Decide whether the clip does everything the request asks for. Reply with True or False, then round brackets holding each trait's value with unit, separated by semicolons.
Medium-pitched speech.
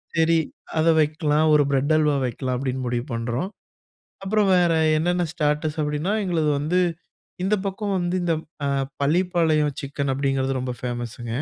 True (150 Hz)